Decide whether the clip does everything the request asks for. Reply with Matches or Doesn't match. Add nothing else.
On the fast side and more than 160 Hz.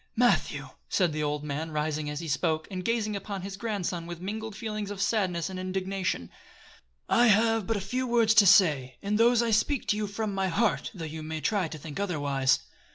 Matches